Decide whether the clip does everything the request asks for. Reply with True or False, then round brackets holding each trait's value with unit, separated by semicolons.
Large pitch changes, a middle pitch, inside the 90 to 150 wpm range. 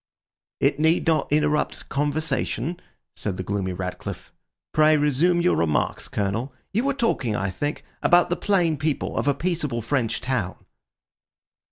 True (6.4 semitones; 145 Hz; 145 wpm)